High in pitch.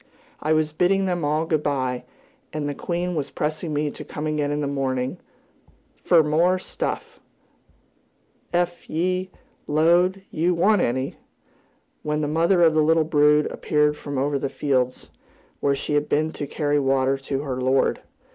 No: medium, 150 Hz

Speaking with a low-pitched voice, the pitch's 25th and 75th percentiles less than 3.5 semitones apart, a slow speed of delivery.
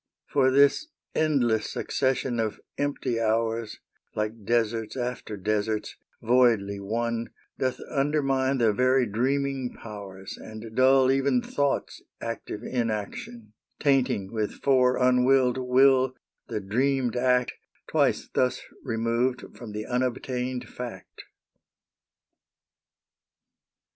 Yes: low, 125 Hz; average, 2.9 semitones; slow, 100 wpm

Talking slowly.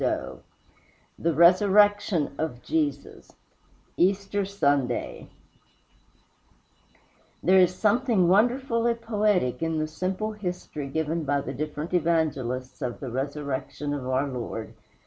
Yes: slow, 110 wpm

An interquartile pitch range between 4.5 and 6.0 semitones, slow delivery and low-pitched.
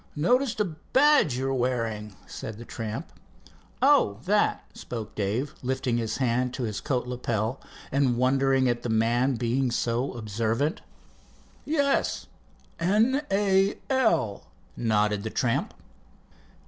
Yes: average, 5.2 semitones; slow, 120 wpm; low, 125 Hz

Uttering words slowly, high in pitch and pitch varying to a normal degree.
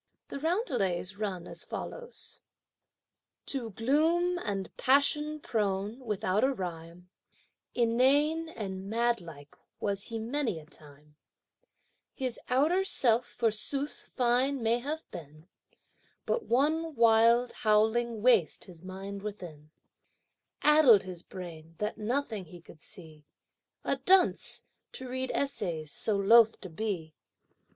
No: slow, 115 wpm; high, 225 Hz; wide, 6.4 semitones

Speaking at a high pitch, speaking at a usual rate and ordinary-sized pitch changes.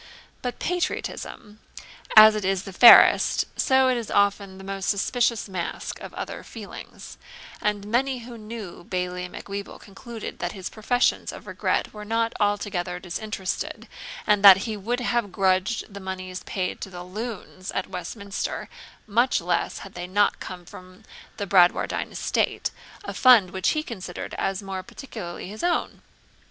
Yes: high, 200 Hz; average, 150 wpm; average, 3.6 semitones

